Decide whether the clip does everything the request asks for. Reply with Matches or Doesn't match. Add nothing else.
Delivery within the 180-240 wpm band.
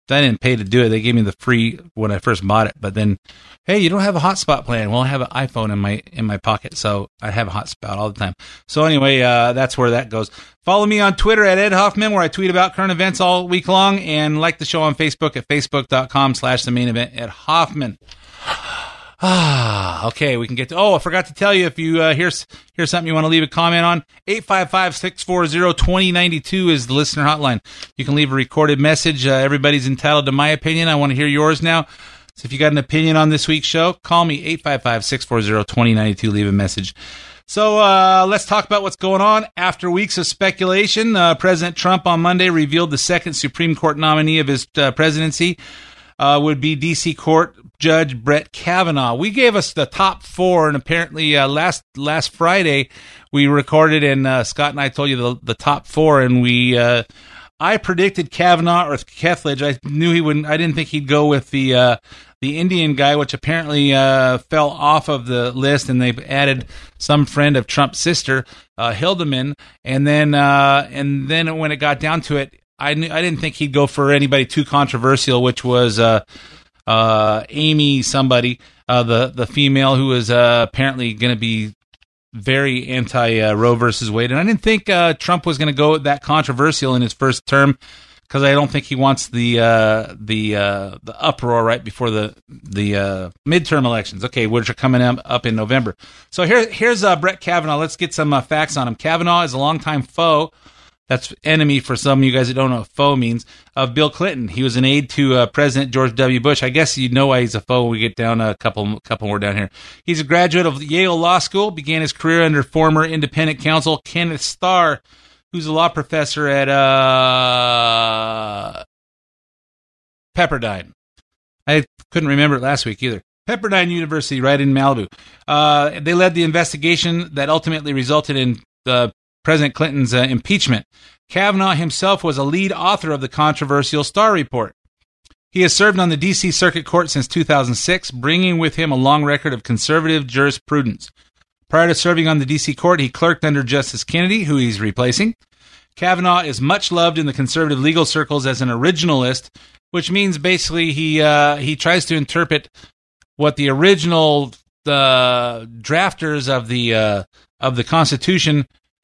Matches